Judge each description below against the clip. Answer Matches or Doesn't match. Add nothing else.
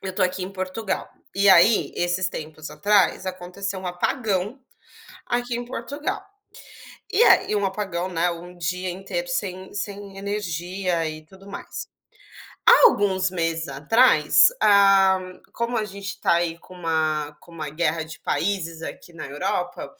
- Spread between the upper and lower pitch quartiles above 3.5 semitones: Doesn't match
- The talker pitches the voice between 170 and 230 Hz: Matches